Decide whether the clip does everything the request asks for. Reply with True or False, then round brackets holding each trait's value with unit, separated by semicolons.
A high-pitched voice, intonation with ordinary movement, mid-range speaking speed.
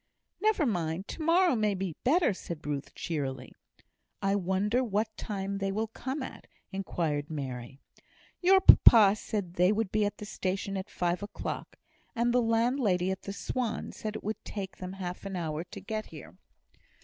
True (195 Hz; 4.0 semitones; 175 wpm)